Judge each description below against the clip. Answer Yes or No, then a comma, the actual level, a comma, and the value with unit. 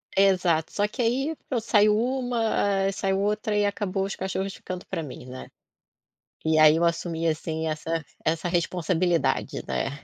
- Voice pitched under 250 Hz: Yes, medium, 185 Hz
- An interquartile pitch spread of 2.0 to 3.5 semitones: No, average, 4.1 semitones